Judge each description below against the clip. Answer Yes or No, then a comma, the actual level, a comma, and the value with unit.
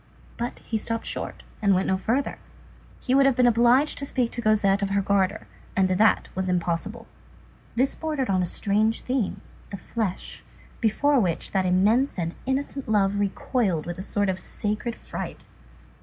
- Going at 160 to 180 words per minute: Yes, average, 170 wpm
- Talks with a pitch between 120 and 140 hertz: No, high, 215 Hz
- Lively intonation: No, average, 4.3 semitones